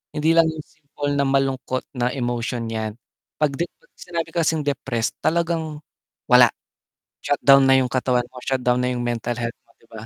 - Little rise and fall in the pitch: No, average, 3.8 semitones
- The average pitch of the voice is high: No, low, 135 Hz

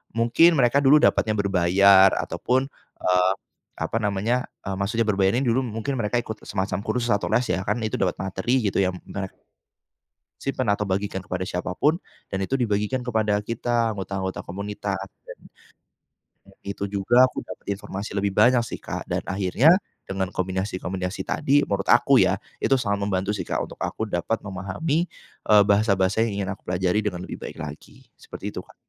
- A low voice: Yes, low, 100 Hz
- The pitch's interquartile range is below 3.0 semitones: No, average, 3.6 semitones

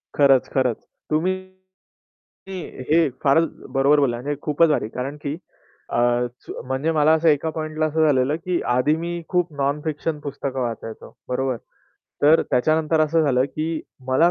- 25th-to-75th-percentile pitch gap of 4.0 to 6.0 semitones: No, average, 3.0 semitones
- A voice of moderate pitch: Yes, medium, 150 Hz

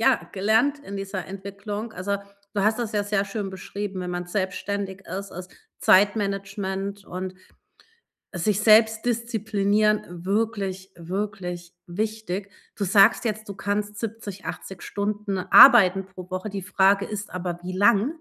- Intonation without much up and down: Yes, narrow, 2.0 semitones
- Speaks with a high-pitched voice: Yes, high, 200 Hz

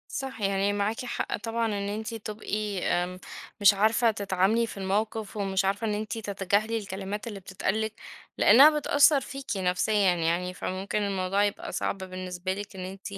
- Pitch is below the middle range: No, high, 205 Hz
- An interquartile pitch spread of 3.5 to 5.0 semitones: No, narrow, 2.4 semitones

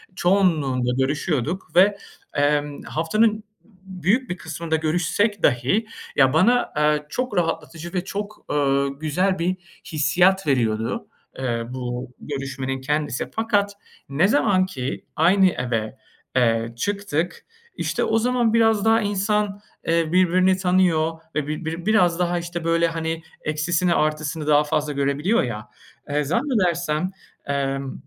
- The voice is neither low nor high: Yes, medium, 165 Hz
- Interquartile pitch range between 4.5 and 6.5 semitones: Yes, average, 4.9 semitones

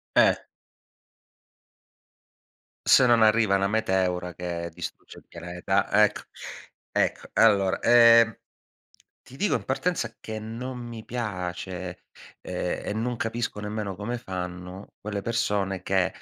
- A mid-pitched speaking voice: No, low, 105 Hz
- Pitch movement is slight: No, average, 4.0 semitones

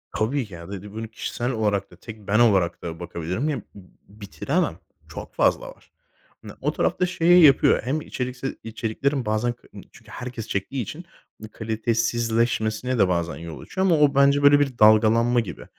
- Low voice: Yes, low, 115 Hz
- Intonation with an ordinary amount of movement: Yes, average, 4.4 semitones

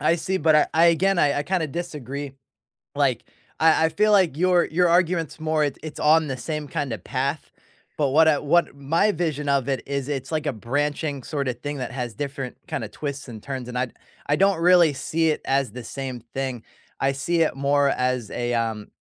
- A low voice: No, medium, 145 Hz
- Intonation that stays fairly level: No, average, 3.4 semitones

